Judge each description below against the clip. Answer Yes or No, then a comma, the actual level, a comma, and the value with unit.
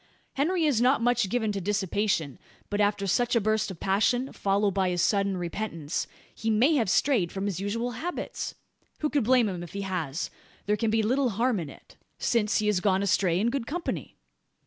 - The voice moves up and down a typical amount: Yes, average, 4.1 semitones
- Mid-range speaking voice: No, high, 210 Hz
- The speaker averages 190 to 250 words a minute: Yes, average, 200 wpm